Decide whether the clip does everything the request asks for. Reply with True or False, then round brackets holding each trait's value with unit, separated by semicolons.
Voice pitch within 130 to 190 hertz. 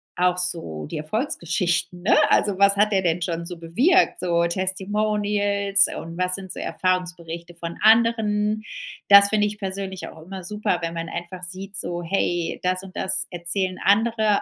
True (185 Hz)